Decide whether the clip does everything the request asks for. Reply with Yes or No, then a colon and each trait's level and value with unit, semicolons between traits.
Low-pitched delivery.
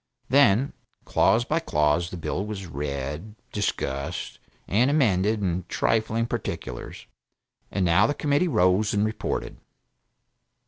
Yes: low, 105 Hz